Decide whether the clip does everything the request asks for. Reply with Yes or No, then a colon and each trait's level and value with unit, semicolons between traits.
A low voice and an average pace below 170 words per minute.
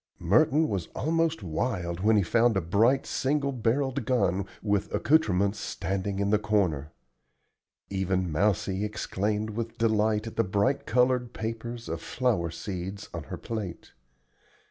Yes: low, 105 Hz; average, 140 wpm